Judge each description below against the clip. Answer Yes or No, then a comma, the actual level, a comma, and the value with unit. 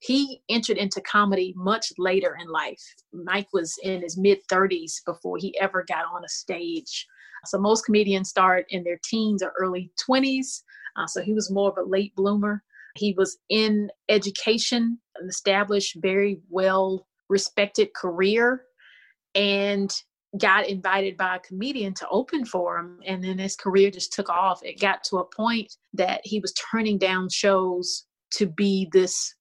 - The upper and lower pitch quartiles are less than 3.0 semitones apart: Yes, narrow, 2.4 semitones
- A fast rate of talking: No, average, 165 wpm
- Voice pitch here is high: Yes, high, 195 Hz